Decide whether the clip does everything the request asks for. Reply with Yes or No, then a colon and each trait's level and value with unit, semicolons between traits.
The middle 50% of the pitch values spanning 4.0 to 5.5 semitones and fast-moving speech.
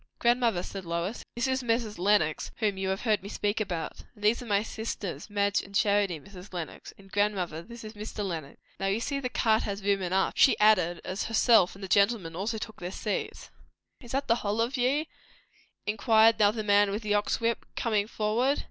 No: average, 2.8 semitones; fast, 210 wpm